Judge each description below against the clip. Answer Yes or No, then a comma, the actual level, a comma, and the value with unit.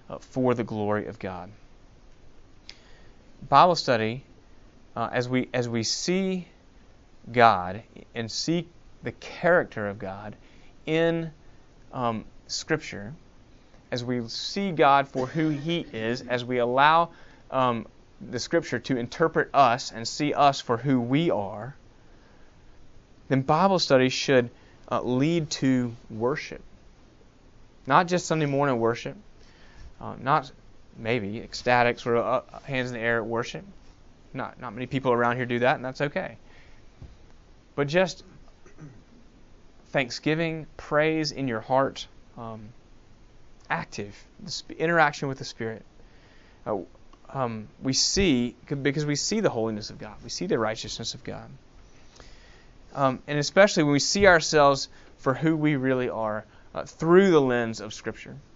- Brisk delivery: No, slow, 135 wpm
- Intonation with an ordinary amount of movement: Yes, average, 4.7 semitones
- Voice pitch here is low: Yes, low, 125 Hz